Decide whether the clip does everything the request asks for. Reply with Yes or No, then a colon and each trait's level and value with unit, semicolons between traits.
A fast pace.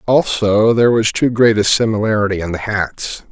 No: average, 180 wpm